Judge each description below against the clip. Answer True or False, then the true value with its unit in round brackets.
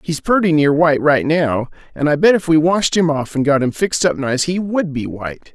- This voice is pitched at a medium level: True (155 Hz)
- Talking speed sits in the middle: False (260 wpm)